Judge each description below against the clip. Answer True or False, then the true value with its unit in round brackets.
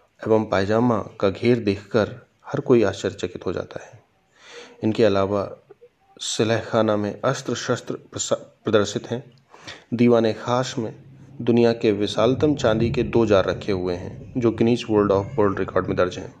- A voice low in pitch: True (115 Hz)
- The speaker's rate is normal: True (150 wpm)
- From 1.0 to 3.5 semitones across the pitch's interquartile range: True (2.9 semitones)